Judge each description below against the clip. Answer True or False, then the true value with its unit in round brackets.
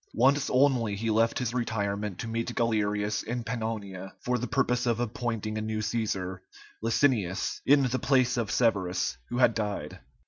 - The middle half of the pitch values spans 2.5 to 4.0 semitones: True (2.8 semitones)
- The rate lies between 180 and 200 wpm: False (165 wpm)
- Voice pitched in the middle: False (115 Hz)